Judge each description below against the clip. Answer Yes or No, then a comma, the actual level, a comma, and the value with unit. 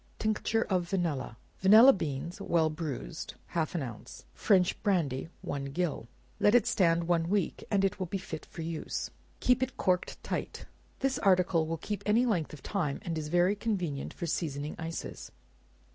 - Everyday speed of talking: Yes, average, 170 wpm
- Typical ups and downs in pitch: Yes, average, 4.1 semitones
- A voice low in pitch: No, medium, 175 Hz